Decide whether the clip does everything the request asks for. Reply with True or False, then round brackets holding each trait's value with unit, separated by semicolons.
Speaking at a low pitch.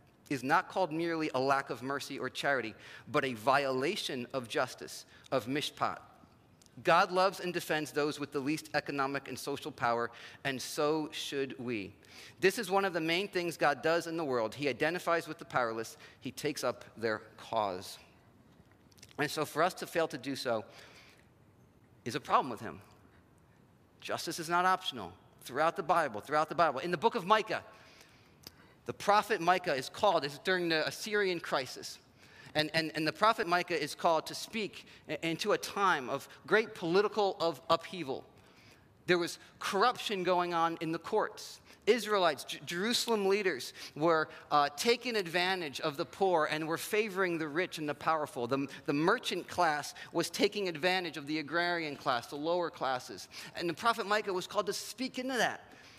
False (165 Hz)